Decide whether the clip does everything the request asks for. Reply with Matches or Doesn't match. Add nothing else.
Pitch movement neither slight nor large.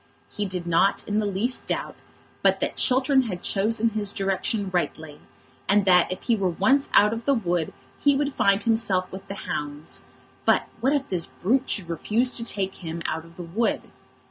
Matches